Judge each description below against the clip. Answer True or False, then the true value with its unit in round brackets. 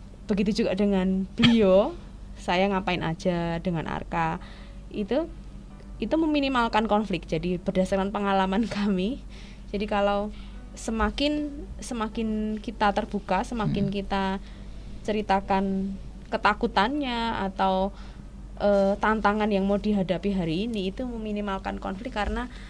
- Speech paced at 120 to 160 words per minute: False (105 wpm)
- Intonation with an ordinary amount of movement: False (2.1 semitones)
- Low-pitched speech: False (205 Hz)